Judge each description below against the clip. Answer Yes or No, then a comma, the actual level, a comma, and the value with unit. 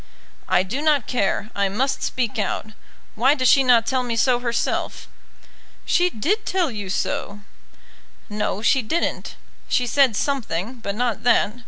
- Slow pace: No, average, 155 wpm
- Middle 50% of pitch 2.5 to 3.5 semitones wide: No, average, 4.2 semitones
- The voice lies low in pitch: No, high, 240 Hz